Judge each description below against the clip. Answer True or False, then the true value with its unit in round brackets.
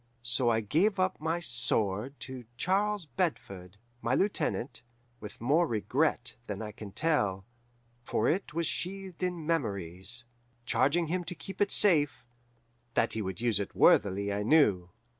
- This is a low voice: True (130 Hz)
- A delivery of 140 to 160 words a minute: True (150 wpm)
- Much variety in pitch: True (8.4 semitones)